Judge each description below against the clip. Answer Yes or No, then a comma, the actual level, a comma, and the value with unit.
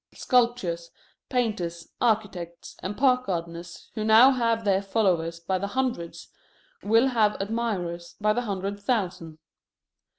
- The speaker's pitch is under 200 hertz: No, high, 205 Hz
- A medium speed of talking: No, slow, 125 wpm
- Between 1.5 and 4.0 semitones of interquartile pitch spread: No, average, 5.2 semitones